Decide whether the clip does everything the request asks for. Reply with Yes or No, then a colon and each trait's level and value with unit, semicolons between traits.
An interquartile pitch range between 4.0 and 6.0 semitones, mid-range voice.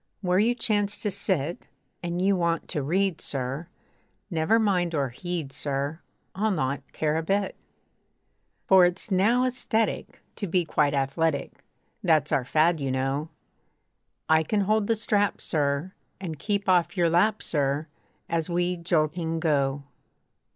Yes: average, 4.7 semitones; medium, 170 Hz